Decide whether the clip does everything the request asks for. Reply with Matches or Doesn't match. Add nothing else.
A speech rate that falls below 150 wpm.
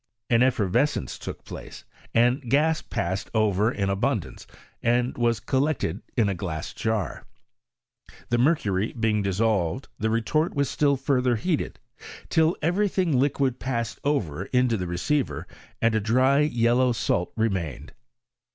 Matches